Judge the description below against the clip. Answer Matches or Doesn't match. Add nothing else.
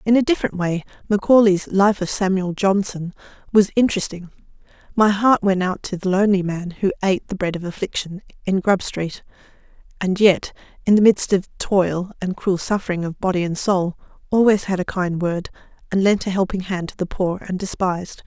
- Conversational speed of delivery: Matches